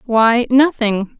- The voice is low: No, high, 235 Hz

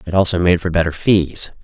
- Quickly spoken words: Yes, fast, 220 wpm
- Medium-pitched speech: No, very low, 85 Hz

